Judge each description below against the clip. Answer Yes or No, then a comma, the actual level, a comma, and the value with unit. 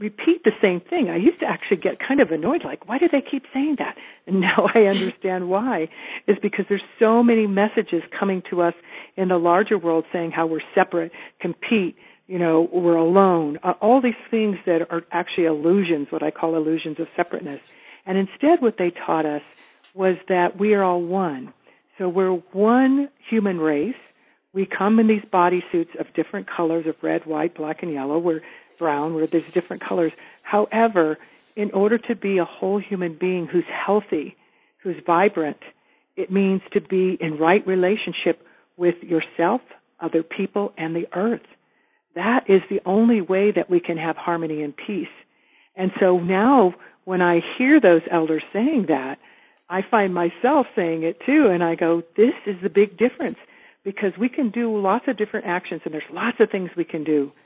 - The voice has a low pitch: No, medium, 185 Hz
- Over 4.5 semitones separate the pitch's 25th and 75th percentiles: No, average, 3.8 semitones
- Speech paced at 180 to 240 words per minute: Yes, average, 185 wpm